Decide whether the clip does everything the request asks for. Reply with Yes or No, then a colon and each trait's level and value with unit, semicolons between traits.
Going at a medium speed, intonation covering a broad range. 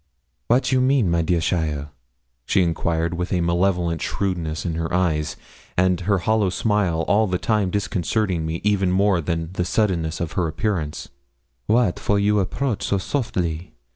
No: average, 165 wpm; average, 3.6 semitones